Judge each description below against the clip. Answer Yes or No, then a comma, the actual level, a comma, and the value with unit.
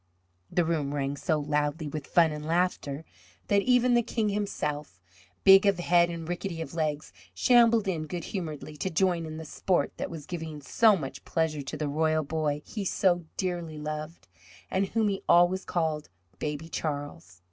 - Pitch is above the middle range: No, medium, 160 Hz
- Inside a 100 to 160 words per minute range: No, average, 175 wpm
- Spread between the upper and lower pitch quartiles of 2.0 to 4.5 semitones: Yes, average, 3.7 semitones